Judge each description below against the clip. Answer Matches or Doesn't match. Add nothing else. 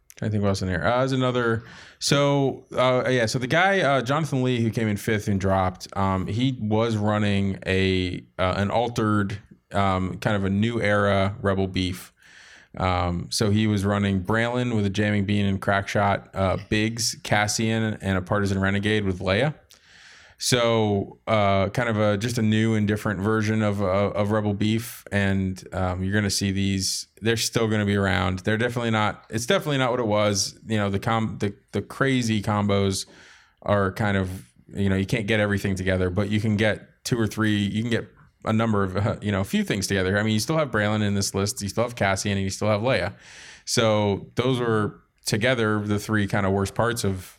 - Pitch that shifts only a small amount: Matches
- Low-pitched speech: Matches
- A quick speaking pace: Matches